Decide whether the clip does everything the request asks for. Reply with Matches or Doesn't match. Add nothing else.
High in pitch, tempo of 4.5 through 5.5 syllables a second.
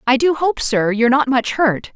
Matches